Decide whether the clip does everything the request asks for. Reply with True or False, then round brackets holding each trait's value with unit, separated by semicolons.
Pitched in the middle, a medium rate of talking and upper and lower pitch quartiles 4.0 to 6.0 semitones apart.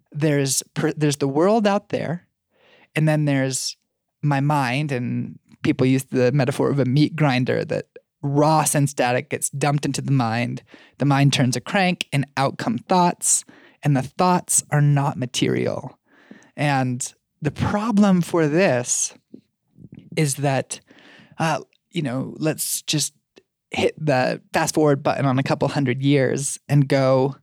False (145 Hz; 150 wpm; 2.7 semitones)